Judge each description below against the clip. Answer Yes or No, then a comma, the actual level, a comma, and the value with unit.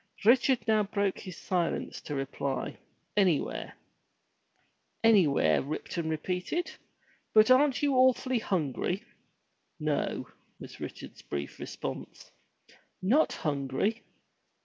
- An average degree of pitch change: No, wide, 7.6 semitones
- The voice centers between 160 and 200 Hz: Yes, medium, 185 Hz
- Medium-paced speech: No, slow, 95 wpm